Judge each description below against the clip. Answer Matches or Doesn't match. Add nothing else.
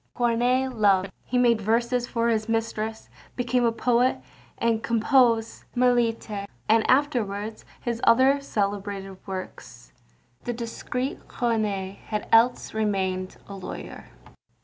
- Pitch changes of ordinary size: Matches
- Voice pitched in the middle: Doesn't match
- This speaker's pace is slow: Matches